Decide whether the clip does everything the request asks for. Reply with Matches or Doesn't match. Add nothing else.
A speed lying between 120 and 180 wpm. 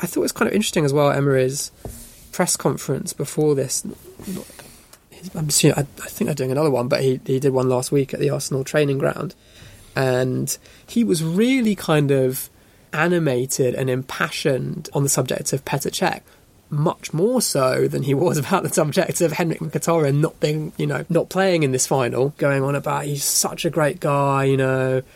Doesn't match